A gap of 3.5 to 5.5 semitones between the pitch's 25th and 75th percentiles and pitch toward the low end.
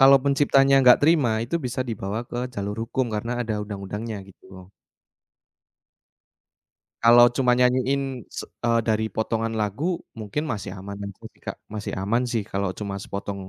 Yes: average, 3.9 semitones; low, 115 Hz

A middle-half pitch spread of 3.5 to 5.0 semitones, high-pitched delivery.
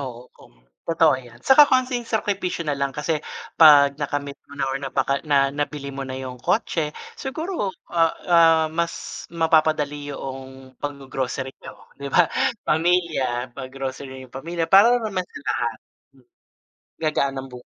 No: average, 3.9 semitones; medium, 145 Hz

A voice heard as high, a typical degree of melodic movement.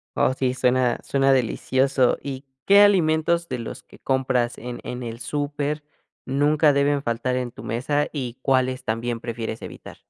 No: low, 130 Hz; average, 3.0 semitones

